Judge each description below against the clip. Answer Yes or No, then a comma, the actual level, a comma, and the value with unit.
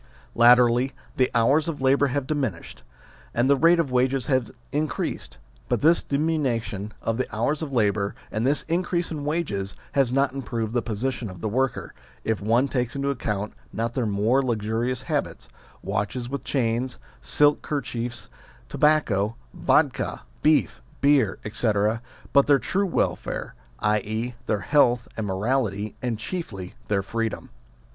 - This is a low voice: Yes, low, 125 Hz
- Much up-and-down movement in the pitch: No, average, 4.3 semitones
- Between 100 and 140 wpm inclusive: No, average, 150 wpm